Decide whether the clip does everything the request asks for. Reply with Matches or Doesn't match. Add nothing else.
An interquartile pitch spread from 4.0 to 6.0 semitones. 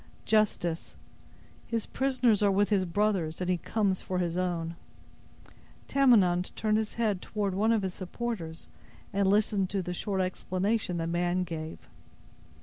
Doesn't match